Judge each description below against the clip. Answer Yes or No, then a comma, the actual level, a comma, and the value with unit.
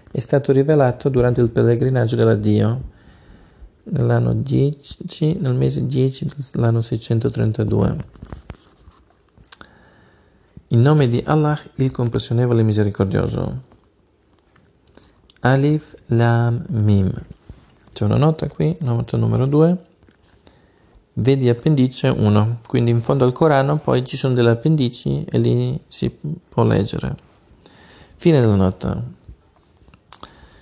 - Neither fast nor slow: No, slow, 100 wpm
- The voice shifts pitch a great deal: No, average, 4.6 semitones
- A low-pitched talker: Yes, low, 120 Hz